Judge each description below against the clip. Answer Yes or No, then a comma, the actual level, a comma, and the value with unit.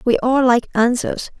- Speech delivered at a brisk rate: No, average, 170 wpm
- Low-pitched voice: No, high, 245 Hz